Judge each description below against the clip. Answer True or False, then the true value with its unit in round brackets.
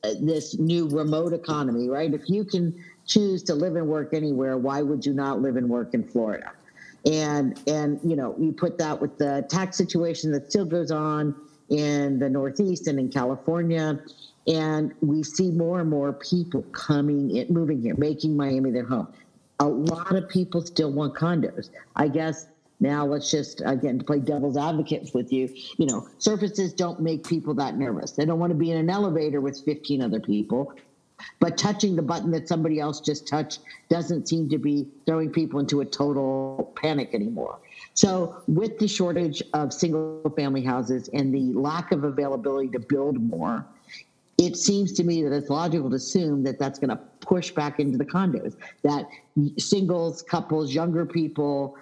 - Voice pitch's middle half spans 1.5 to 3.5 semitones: True (2.9 semitones)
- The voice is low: False (155 Hz)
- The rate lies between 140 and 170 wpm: False (180 wpm)